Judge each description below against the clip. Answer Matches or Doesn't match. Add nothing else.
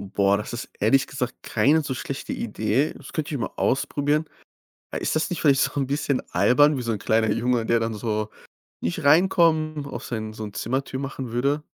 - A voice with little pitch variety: Doesn't match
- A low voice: Matches